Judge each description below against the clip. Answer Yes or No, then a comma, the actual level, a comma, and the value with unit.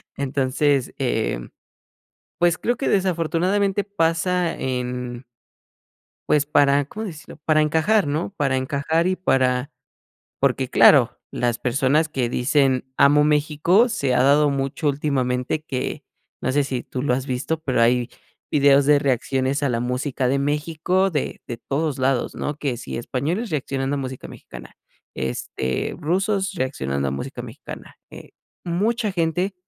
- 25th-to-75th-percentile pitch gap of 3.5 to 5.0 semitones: Yes, average, 4.1 semitones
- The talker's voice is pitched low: No, medium, 145 Hz